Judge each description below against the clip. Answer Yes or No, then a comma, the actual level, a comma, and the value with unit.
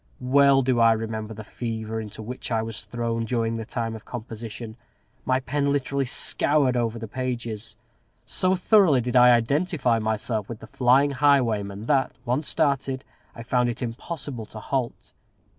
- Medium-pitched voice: No, low, 120 Hz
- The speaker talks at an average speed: Yes, average, 160 wpm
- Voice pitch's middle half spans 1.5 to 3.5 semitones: Yes, average, 3.2 semitones